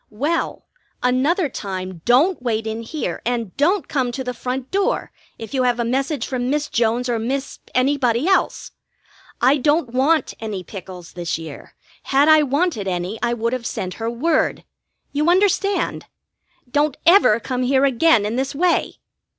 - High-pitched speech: Yes, very high, 255 Hz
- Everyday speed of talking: Yes, average, 165 wpm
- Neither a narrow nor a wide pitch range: Yes, average, 4.5 semitones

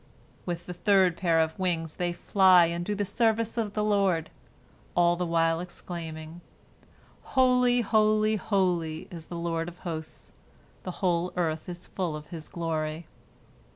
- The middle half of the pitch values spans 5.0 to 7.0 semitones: No, average, 3.3 semitones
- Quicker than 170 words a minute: No, average, 155 wpm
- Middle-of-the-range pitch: Yes, medium, 175 Hz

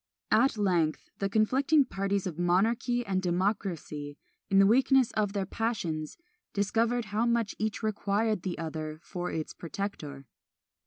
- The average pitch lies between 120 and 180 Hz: No, high, 200 Hz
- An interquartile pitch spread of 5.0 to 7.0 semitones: No, average, 4.2 semitones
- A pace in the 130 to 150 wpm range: Yes, average, 140 wpm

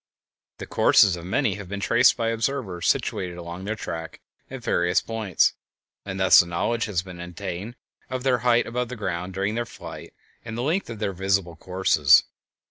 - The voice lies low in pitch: Yes, low, 100 Hz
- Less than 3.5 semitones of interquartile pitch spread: No, average, 4.8 semitones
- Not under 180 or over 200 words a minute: Yes, average, 190 wpm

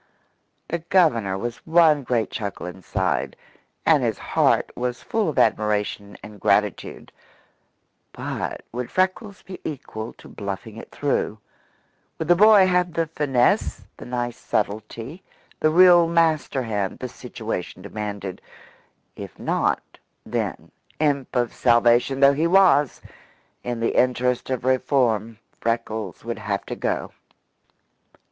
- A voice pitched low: Yes, low, 125 Hz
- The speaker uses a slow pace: Yes, slow, 125 wpm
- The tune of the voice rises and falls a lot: Yes, wide, 6.4 semitones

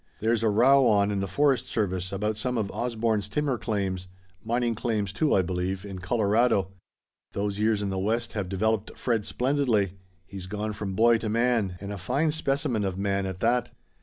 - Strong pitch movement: No, average, 3.2 semitones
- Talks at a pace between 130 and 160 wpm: No, average, 190 wpm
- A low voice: Yes, low, 105 Hz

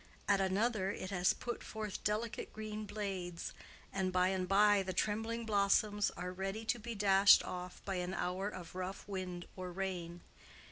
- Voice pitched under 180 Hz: No, high, 195 Hz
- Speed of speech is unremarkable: Yes, average, 170 wpm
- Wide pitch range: No, narrow, 2.4 semitones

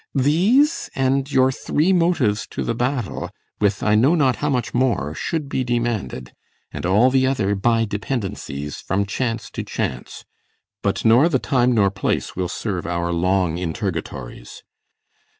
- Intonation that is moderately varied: No, wide, 5.8 semitones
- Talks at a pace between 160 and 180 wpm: No, average, 150 wpm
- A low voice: Yes, low, 115 Hz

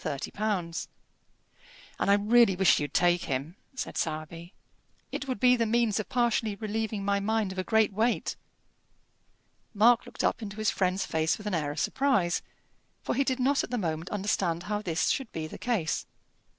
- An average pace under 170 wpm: No, average, 175 wpm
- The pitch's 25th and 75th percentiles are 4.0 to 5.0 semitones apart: Yes, average, 4.7 semitones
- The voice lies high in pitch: Yes, high, 205 Hz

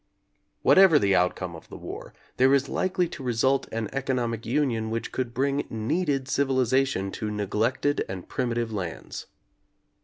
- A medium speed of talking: Yes, average, 145 wpm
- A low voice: Yes, low, 125 Hz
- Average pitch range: Yes, average, 3.9 semitones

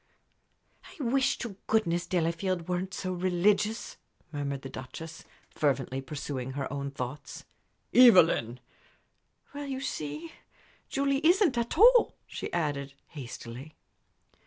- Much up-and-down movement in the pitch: Yes, wide, 8.9 semitones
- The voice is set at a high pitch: No, medium, 170 Hz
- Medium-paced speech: No, slow, 110 wpm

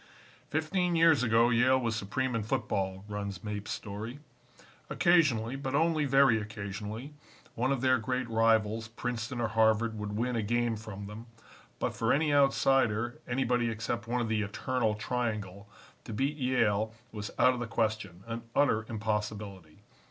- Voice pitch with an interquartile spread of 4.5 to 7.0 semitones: No, average, 3.2 semitones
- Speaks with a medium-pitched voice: No, low, 115 Hz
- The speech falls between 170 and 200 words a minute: No, average, 155 wpm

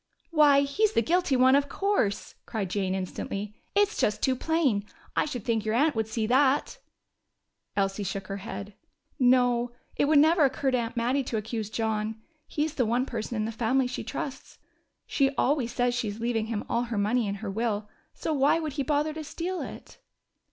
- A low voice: No, high, 245 Hz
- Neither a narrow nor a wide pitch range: Yes, average, 4.7 semitones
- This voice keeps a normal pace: Yes, average, 195 wpm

